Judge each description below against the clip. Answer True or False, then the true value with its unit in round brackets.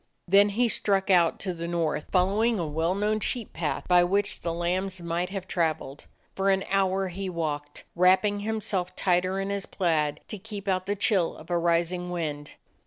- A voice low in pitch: False (185 Hz)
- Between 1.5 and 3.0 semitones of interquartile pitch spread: True (2.7 semitones)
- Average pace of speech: True (185 wpm)